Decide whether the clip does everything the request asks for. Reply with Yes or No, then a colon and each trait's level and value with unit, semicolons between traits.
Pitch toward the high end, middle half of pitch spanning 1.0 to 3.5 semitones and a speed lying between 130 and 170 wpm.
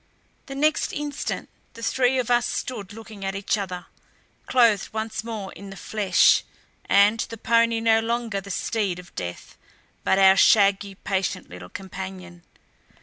Yes: high, 205 Hz; average, 3.1 semitones; average, 150 wpm